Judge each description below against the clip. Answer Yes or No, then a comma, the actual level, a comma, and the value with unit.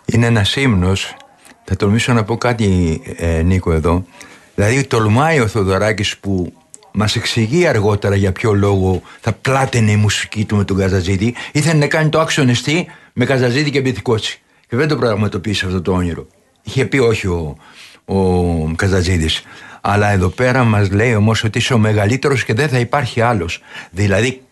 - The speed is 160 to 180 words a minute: Yes, average, 165 wpm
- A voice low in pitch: Yes, low, 105 Hz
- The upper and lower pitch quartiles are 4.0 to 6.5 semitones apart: Yes, average, 4.5 semitones